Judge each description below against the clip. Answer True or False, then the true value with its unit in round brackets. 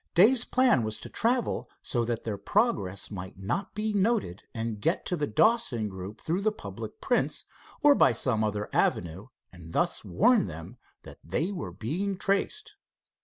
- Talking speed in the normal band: True (170 wpm)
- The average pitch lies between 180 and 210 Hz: False (120 Hz)